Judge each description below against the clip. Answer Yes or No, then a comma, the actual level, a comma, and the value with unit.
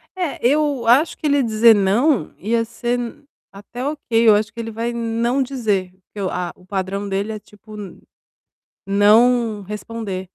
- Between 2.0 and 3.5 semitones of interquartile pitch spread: Yes, average, 3.2 semitones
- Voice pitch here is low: No, high, 225 Hz